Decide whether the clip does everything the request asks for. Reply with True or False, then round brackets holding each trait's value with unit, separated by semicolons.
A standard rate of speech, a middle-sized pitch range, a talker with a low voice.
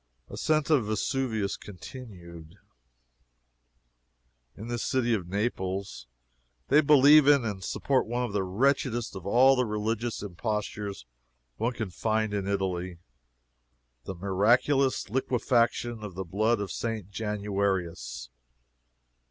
False (115 wpm; 4.1 semitones; 105 Hz)